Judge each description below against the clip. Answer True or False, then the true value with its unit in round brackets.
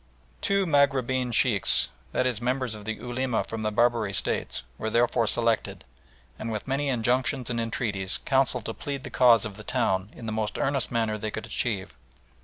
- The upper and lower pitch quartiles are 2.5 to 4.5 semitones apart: True (2.9 semitones)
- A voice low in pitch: True (115 Hz)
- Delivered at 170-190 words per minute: True (185 wpm)